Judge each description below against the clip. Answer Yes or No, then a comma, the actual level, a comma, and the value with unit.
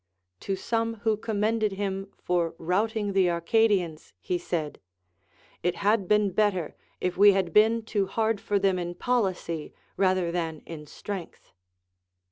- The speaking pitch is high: Yes, high, 195 Hz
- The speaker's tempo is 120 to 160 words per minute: Yes, average, 140 wpm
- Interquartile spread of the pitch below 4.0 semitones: Yes, average, 3.3 semitones